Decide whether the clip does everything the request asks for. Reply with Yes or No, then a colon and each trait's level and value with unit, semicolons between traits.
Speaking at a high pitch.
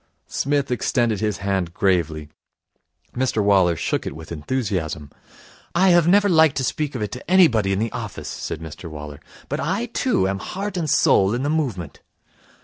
No: low, 110 Hz